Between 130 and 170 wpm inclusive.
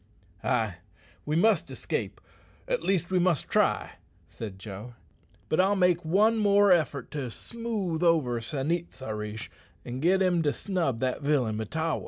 Yes: average, 160 wpm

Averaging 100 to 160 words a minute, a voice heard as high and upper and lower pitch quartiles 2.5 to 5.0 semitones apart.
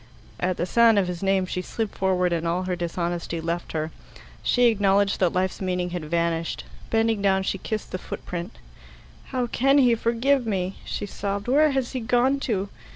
No: average, 185 wpm; high, 195 Hz; average, 4.5 semitones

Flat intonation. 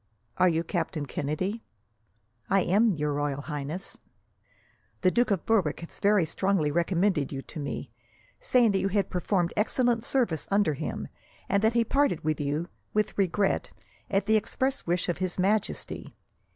No: average, 5.0 semitones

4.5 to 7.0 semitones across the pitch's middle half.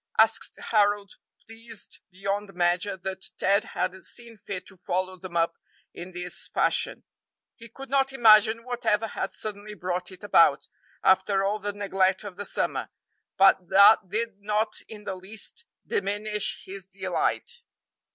No: narrow, 2.5 semitones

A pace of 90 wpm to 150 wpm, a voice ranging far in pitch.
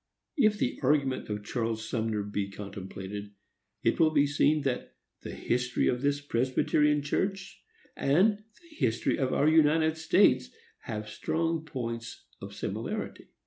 Yes: average, 140 wpm; wide, 5.7 semitones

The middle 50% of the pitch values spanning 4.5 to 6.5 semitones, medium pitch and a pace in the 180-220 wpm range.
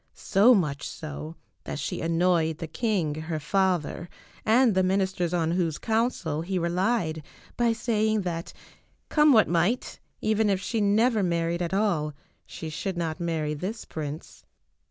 No: average, 4.8 semitones; medium, 180 Hz; average, 150 wpm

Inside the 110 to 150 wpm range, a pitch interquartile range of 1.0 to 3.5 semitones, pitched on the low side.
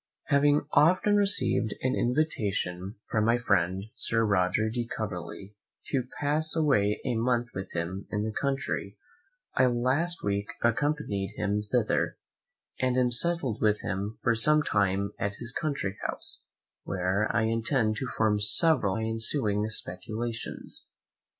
No: average, 140 wpm; average, 4.4 semitones; low, 110 Hz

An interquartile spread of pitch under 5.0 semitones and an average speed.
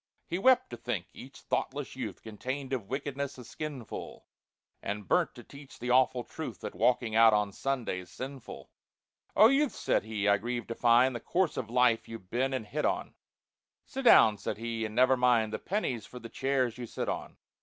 Yes: average, 3.2 semitones; average, 195 wpm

